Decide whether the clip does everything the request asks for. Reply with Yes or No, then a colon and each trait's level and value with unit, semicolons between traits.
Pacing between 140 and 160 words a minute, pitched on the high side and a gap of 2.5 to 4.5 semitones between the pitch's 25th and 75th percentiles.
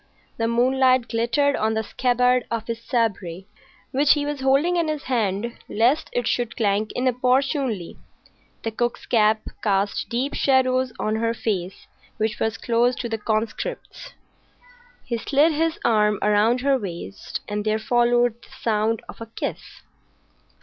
Yes: average, 150 wpm; high, 235 Hz; average, 3.0 semitones